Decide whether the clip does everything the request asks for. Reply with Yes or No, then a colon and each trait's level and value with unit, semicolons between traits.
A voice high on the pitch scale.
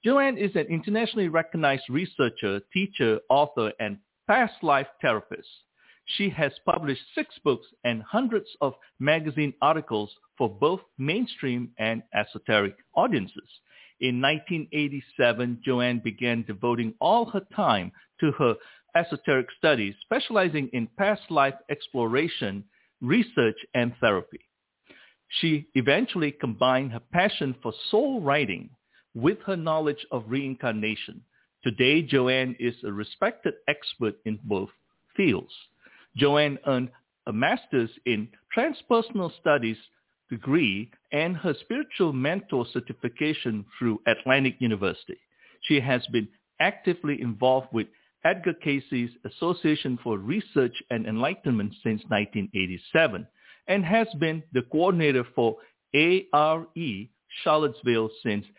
No: low, 135 Hz